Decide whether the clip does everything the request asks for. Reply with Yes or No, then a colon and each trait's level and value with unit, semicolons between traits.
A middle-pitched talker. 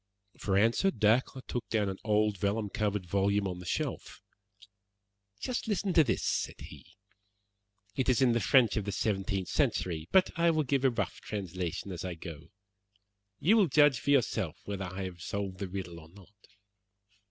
No: low, 105 Hz